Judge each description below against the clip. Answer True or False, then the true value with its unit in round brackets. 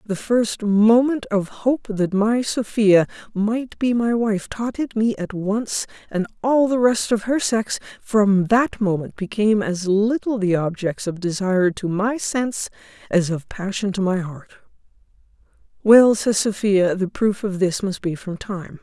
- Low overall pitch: False (210 Hz)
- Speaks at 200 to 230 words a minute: False (170 wpm)